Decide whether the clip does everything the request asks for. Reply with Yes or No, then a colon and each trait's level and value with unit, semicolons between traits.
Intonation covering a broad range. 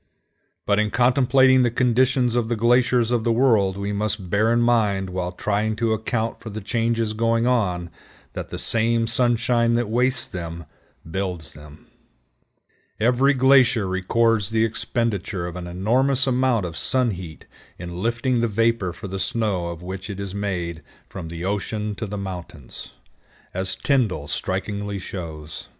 No: average, 4.1 semitones